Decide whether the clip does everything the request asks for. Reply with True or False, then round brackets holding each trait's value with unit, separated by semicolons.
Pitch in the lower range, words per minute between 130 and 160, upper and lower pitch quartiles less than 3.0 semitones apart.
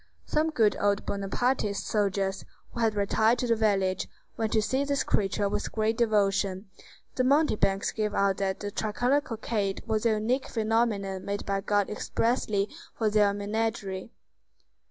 False (210 Hz; 155 wpm; 2.4 semitones)